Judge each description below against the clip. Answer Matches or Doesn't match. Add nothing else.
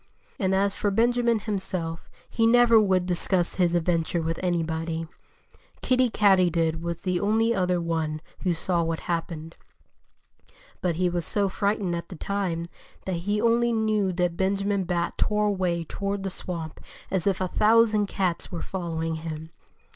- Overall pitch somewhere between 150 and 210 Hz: Matches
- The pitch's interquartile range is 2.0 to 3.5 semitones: Matches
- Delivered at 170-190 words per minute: Doesn't match